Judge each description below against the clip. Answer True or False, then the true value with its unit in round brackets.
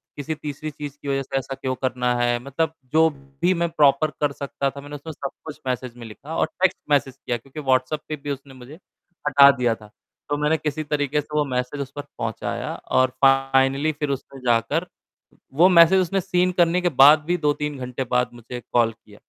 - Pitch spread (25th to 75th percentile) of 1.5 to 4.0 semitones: True (2.9 semitones)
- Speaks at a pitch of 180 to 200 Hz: False (140 Hz)